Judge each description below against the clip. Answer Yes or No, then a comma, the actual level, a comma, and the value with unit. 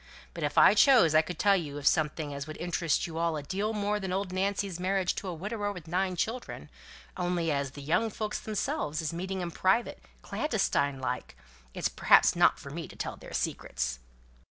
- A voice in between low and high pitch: Yes, medium, 180 Hz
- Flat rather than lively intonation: No, average, 4.2 semitones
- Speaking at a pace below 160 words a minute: No, average, 200 wpm